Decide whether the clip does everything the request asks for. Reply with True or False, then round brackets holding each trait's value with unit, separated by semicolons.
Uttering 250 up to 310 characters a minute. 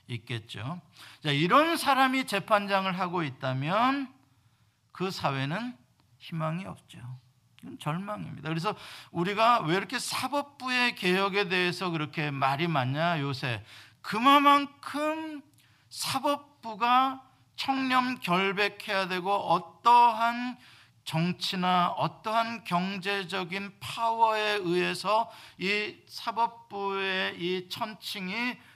False (225 characters per minute)